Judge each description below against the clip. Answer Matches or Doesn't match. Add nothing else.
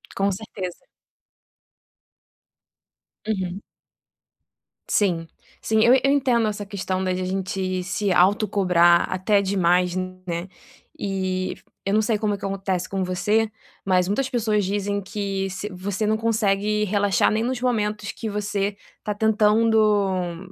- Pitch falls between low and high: Doesn't match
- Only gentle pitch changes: Matches